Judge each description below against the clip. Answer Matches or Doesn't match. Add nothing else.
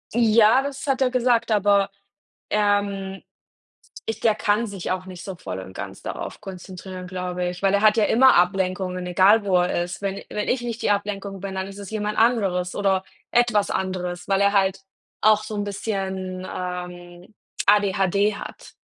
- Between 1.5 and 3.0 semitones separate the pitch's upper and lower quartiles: Matches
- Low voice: Doesn't match